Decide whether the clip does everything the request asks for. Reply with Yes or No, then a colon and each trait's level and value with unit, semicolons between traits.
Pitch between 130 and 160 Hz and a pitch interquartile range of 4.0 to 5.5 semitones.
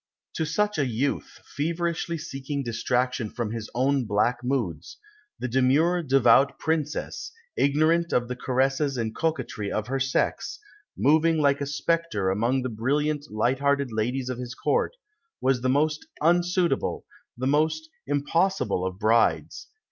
Yes: low, 135 Hz; average, 4.3 semitones